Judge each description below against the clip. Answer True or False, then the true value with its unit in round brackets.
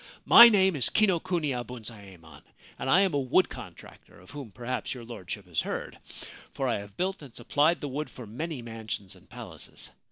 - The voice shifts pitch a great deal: True (6.7 semitones)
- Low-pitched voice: True (125 Hz)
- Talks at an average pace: True (185 wpm)